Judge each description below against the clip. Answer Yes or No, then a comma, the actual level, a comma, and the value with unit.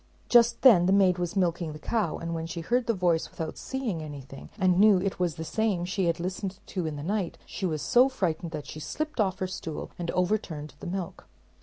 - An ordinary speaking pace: No, fast, 225 wpm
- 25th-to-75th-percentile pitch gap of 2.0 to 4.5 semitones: Yes, average, 3.6 semitones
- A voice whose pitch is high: No, medium, 180 Hz